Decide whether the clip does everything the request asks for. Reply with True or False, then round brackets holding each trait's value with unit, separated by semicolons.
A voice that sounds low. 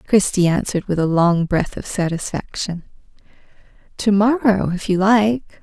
False (195 Hz)